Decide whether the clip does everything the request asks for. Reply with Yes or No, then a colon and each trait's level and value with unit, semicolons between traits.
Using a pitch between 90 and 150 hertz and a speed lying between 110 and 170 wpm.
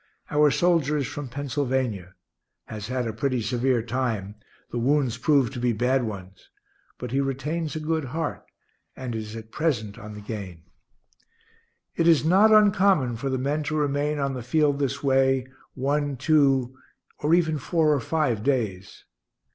Yes: low, 135 Hz; average, 165 wpm